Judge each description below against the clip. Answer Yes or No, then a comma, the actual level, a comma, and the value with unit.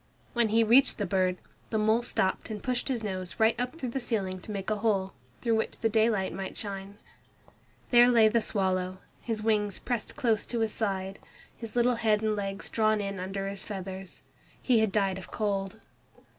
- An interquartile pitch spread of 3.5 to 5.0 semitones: No, average, 2.8 semitones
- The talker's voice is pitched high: Yes, high, 215 Hz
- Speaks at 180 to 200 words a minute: Yes, average, 195 wpm